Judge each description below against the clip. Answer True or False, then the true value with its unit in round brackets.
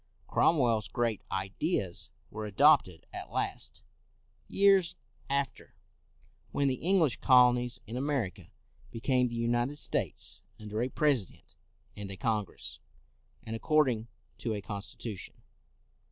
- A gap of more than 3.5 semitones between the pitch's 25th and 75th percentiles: True (4.6 semitones)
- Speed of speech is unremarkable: False (110 wpm)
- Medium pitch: False (120 Hz)